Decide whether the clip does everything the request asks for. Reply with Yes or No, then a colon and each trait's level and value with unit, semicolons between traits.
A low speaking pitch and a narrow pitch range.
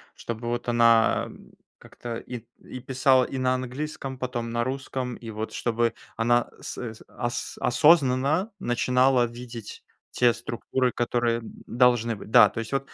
Yes: low, 120 Hz; narrow, 1.7 semitones